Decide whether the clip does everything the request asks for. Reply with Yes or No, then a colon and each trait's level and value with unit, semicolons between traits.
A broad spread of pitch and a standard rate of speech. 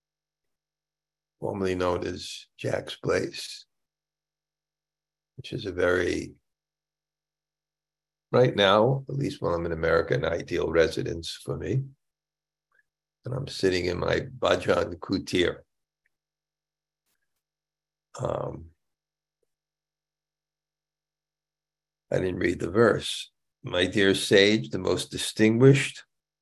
No: wide, 6.0 semitones; slow, 95 wpm